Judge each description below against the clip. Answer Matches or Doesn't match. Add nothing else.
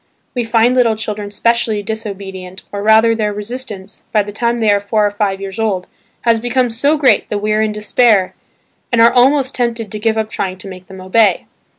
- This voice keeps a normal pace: Doesn't match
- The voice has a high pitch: Matches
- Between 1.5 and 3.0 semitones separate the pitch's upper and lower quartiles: Matches